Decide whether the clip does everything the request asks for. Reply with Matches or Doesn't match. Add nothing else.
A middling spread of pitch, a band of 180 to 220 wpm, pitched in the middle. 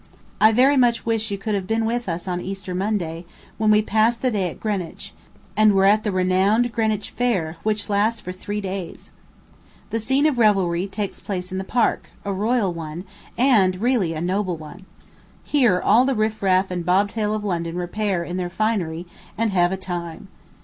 Doesn't match